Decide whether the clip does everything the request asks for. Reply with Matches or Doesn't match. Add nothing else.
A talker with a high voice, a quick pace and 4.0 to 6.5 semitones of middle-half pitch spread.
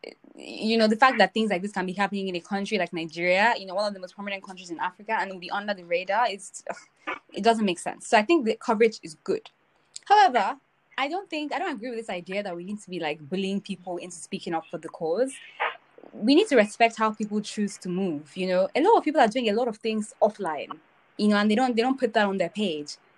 Matches